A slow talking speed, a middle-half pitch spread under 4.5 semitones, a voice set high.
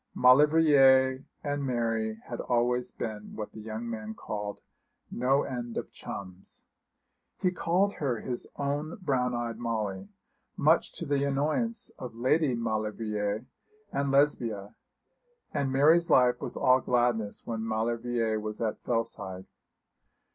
No: slow, 125 wpm; average, 4.0 semitones; low, 120 Hz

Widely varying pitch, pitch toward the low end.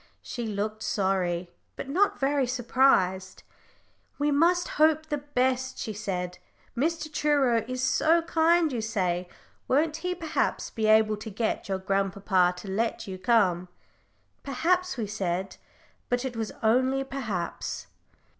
No: wide, 6.8 semitones; high, 235 Hz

